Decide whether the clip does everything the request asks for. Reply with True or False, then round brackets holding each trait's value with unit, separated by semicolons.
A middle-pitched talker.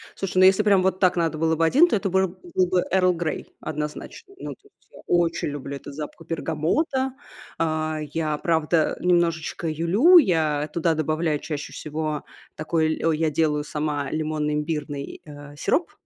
True (160 Hz)